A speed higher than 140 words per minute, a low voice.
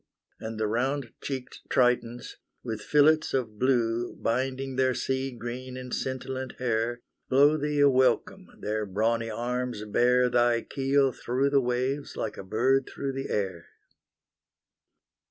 No: slow, 135 wpm; low, 125 Hz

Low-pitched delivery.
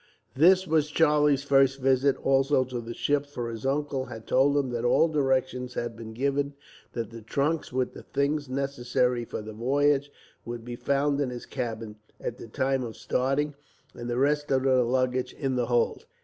Yes: low, 130 Hz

